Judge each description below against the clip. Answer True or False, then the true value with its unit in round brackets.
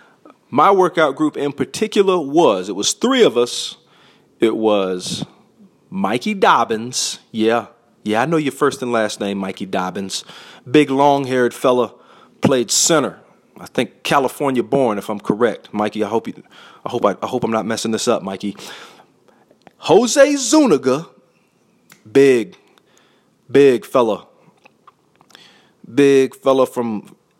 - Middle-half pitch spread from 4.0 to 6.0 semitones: True (5.2 semitones)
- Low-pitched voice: True (130 Hz)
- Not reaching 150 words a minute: True (135 wpm)